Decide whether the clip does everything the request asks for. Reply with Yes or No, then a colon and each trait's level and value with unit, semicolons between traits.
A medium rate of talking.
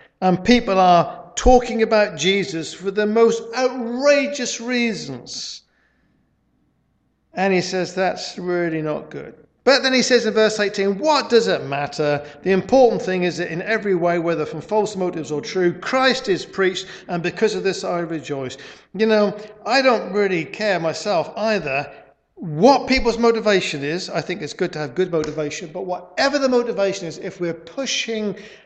Yes: average, 170 wpm